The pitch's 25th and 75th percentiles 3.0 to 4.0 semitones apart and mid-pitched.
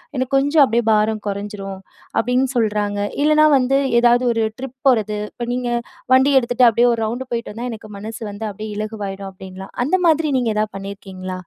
No: average, 3.5 semitones; high, 225 Hz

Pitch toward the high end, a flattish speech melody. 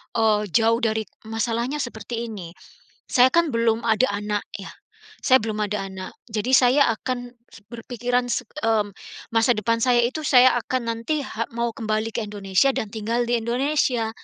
Yes: high, 230 Hz; narrow, 2.3 semitones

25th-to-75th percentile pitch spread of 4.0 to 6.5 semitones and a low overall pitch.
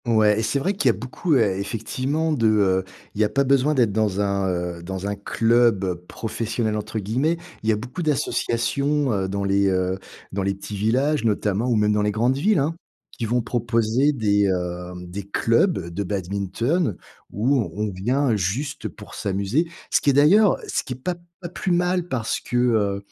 Yes: average, 5.3 semitones; low, 110 Hz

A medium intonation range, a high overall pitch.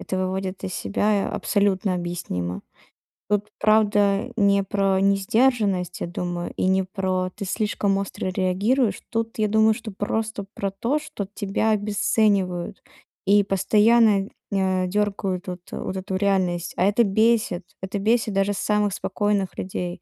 No: narrow, 2.1 semitones; high, 200 Hz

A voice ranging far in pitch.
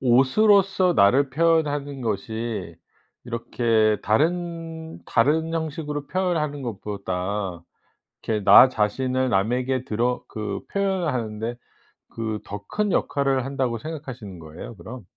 Yes: wide, 6.5 semitones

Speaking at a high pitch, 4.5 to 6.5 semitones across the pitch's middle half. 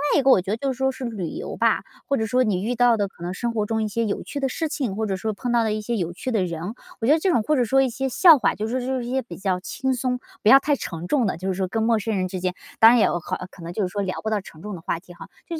Yes: high, 220 Hz; average, 5.1 semitones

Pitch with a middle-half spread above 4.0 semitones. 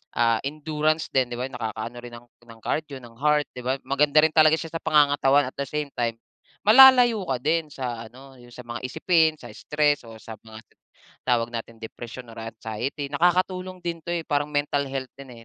Yes: average, 4.5 semitones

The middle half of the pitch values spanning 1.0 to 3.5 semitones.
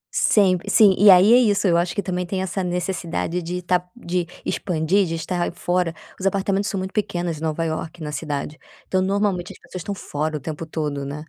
Yes: average, 2.9 semitones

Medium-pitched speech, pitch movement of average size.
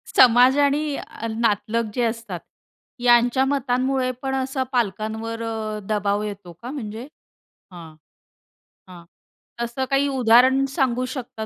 No: high, 240 Hz; average, 3.3 semitones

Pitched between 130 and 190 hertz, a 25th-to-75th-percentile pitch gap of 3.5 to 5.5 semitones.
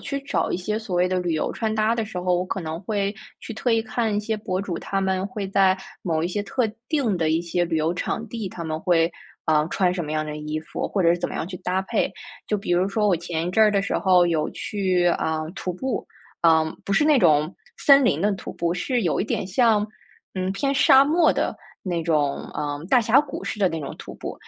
Yes: medium, 185 Hz; average, 4.3 semitones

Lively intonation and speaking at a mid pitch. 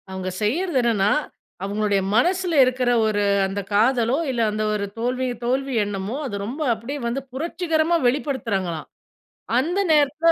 No: wide, 5.8 semitones; very high, 250 Hz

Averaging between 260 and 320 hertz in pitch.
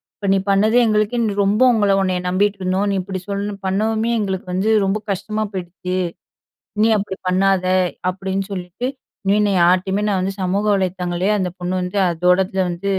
No: high, 195 Hz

